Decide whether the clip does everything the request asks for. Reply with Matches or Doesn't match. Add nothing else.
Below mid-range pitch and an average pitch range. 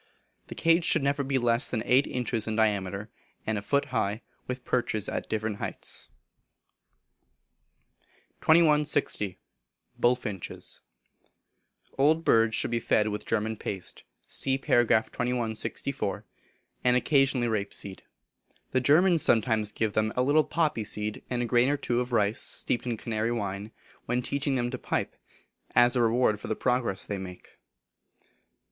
Matches